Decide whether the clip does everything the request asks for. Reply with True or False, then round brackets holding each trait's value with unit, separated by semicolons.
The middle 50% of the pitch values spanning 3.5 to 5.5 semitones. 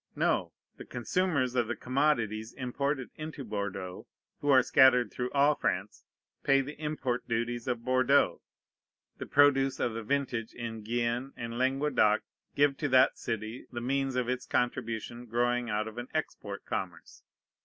False (2.8 semitones)